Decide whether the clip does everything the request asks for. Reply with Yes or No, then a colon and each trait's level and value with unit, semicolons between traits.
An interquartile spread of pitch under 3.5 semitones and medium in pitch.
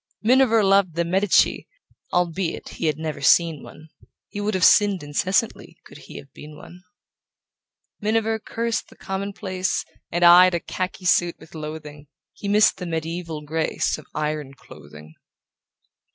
No: average, 4.3 semitones; medium, 175 Hz